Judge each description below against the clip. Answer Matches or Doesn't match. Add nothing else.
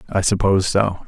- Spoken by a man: Matches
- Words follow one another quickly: Doesn't match